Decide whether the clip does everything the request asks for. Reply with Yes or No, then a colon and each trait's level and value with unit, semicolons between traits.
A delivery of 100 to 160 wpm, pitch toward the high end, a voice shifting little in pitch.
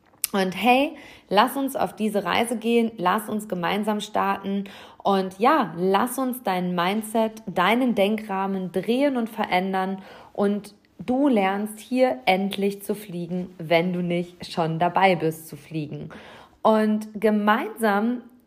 No: average, 130 wpm; high, 200 Hz; average, 3.3 semitones